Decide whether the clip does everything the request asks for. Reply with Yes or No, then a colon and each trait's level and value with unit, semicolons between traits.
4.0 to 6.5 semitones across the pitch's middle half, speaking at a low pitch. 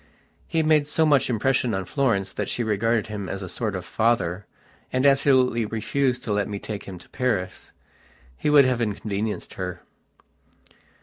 Yes: average, 4.5 semitones; low, 110 Hz